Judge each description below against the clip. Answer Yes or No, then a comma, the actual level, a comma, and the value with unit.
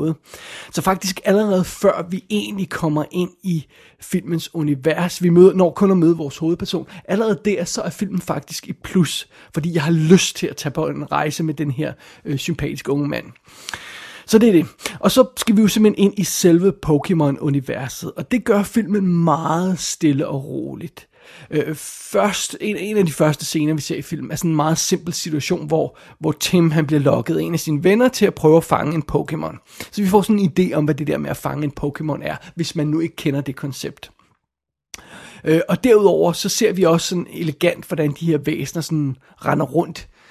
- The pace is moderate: Yes, average, 210 wpm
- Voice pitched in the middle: Yes, medium, 165 Hz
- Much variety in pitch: No, average, 3.8 semitones